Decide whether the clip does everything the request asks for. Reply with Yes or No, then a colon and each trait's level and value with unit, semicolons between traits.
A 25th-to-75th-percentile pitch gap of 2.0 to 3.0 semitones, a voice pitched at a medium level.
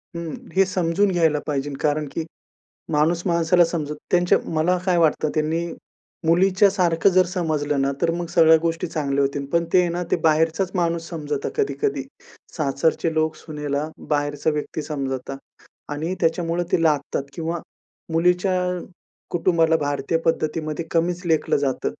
Yes: narrow, 2.6 semitones; medium, 165 Hz